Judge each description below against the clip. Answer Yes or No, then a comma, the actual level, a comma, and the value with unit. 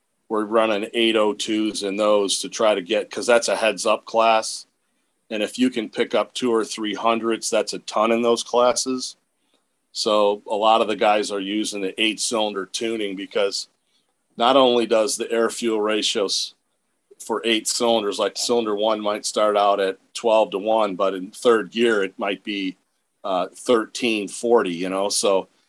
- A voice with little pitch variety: Yes, narrow, 2.0 semitones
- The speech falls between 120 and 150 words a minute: No, average, 180 wpm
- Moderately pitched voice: No, low, 110 Hz